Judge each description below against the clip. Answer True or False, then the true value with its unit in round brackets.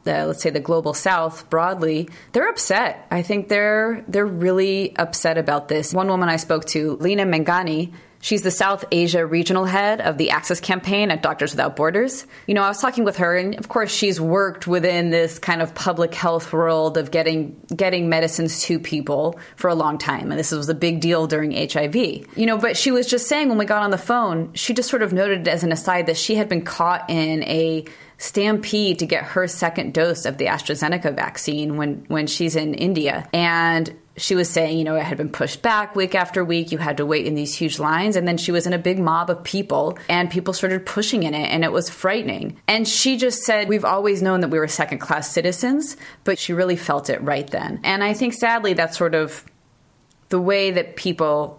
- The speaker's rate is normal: False (220 wpm)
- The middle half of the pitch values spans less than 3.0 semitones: False (3.5 semitones)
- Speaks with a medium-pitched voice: True (175 Hz)